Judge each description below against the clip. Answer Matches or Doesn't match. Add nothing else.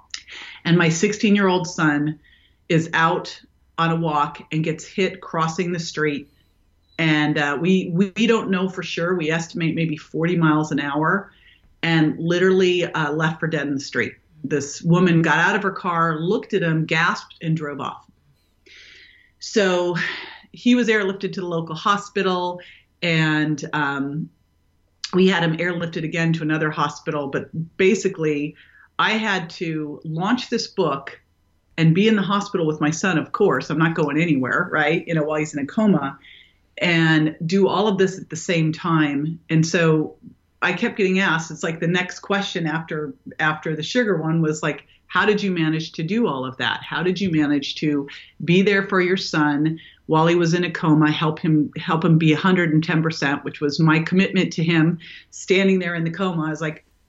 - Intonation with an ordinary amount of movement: Matches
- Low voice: Doesn't match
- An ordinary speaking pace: Matches